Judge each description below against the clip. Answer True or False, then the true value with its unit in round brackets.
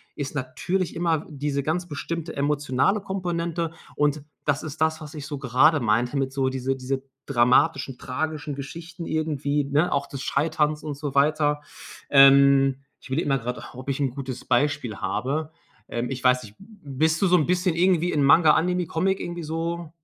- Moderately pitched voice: True (145 Hz)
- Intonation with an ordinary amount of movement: True (3.1 semitones)